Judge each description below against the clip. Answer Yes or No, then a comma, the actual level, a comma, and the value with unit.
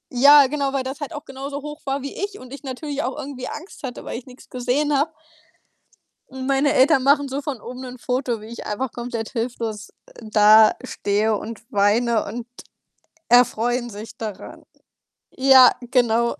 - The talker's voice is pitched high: Yes, very high, 255 Hz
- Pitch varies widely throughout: No, average, 3.2 semitones